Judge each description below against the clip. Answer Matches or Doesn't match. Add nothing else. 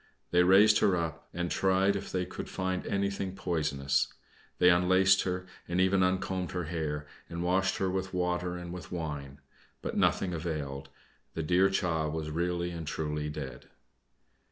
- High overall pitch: Doesn't match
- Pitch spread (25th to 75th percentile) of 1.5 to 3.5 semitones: Matches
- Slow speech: Doesn't match